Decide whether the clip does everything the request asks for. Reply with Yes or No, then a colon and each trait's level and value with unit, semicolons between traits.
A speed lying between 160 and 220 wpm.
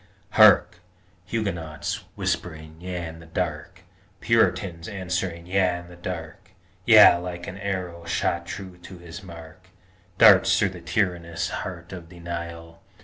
No: average, 140 wpm